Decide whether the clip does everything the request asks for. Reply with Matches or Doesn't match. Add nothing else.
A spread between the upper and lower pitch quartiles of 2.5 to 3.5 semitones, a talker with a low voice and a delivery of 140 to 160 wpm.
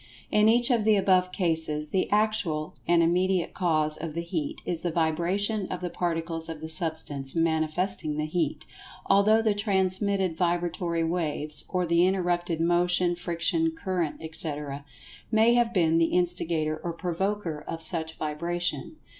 Doesn't match